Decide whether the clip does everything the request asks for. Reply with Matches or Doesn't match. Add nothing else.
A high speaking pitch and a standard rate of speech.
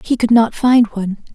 Doesn't match